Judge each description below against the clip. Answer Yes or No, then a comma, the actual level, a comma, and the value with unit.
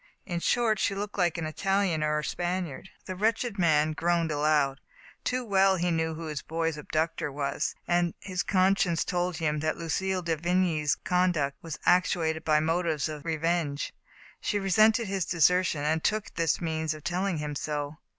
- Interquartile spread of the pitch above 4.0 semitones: No, average, 3.1 semitones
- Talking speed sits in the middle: Yes, average, 180 wpm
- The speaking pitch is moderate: Yes, medium, 170 Hz